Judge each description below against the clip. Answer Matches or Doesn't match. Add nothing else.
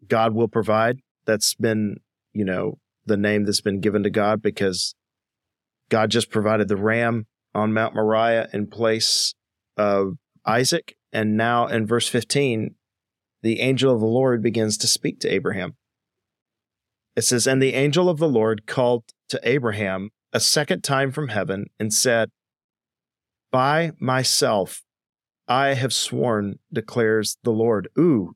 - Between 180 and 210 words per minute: Doesn't match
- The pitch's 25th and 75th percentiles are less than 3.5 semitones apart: Matches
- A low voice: Matches